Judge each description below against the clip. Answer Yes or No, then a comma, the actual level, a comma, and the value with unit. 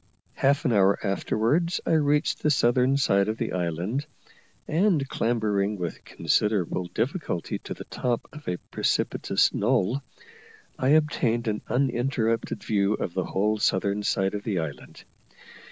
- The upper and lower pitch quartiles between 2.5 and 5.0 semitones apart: No, wide, 5.6 semitones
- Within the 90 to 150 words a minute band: Yes, average, 140 wpm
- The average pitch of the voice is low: Yes, low, 110 Hz